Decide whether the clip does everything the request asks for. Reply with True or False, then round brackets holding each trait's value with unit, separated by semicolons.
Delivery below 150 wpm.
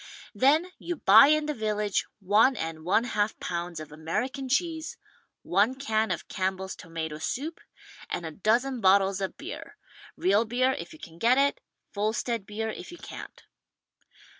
False (165 wpm)